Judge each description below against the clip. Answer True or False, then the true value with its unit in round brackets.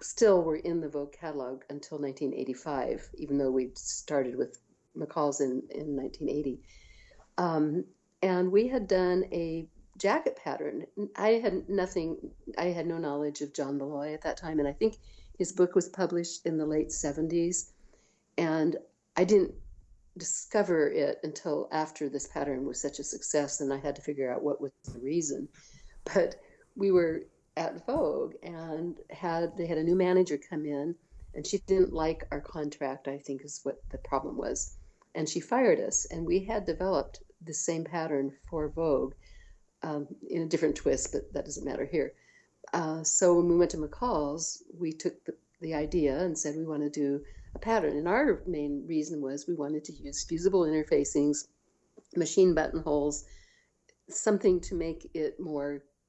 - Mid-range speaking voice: True (160 Hz)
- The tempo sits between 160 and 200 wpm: True (170 wpm)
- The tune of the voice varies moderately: True (3.5 semitones)